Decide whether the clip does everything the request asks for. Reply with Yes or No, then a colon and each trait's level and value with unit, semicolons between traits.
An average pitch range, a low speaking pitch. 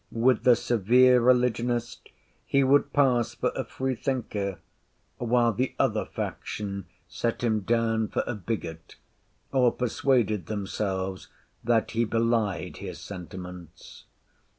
Yes: average, 3.6 semitones; low, 115 Hz